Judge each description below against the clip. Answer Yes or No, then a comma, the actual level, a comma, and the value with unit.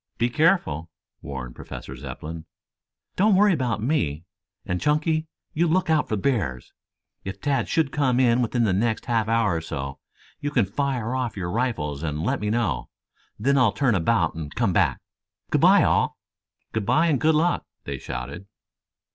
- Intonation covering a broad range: Yes, wide, 9.0 semitones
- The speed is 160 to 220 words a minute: Yes, average, 170 wpm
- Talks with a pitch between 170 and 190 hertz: No, low, 115 Hz